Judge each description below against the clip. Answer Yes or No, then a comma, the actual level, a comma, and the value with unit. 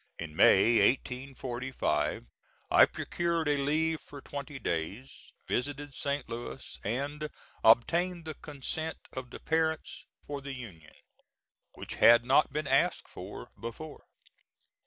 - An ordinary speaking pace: No, slow, 120 wpm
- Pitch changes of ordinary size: Yes, average, 4.1 semitones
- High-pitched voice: No, medium, 140 Hz